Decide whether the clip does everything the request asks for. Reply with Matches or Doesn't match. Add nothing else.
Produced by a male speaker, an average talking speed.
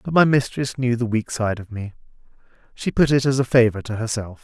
Doesn't match